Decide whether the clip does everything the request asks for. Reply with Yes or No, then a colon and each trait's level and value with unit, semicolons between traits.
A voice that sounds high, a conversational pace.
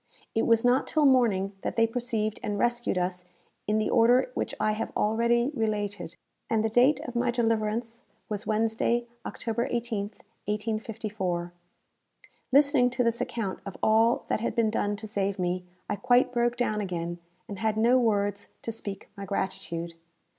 Yes: high, 220 Hz; average, 165 wpm